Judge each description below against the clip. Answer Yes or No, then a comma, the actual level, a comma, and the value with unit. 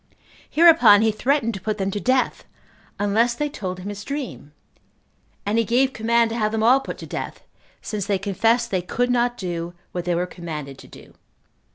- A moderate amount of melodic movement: Yes, average, 4.3 semitones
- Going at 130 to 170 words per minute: No, average, 195 wpm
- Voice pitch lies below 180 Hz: No, high, 215 Hz